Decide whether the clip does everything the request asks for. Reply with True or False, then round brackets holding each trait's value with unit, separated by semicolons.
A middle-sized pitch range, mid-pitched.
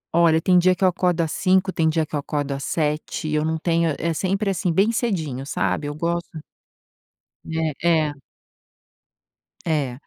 True (3.0 semitones; 165 Hz)